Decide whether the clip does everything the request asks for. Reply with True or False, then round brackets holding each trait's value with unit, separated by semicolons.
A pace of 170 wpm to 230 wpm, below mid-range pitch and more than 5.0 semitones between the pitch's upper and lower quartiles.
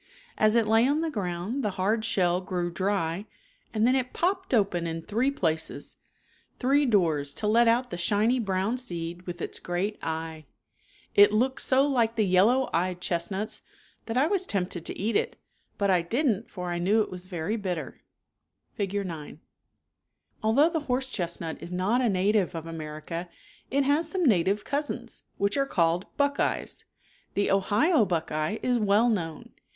False (175 wpm; 205 Hz; 5.6 semitones)